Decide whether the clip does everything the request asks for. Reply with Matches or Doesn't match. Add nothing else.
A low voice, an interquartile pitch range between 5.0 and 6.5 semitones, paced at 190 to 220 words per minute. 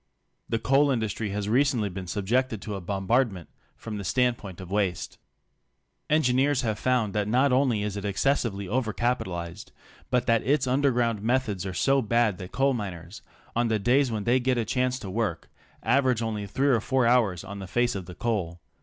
Doesn't match